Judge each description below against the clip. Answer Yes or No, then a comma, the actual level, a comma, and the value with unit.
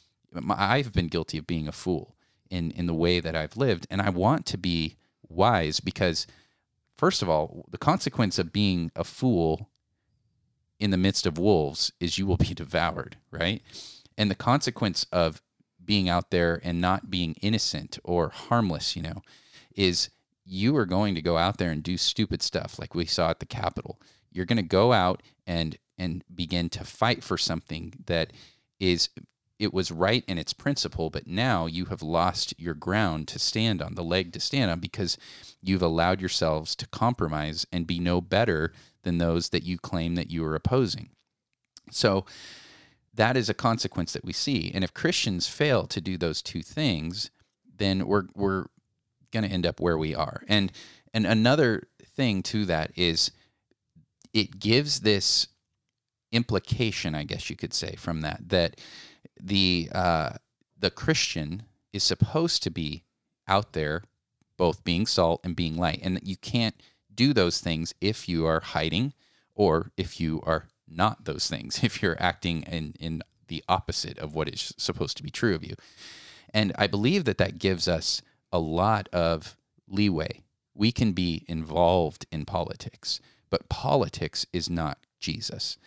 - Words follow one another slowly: No, average, 170 wpm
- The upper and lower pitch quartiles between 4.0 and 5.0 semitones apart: Yes, average, 4.3 semitones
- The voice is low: Yes, very low, 95 Hz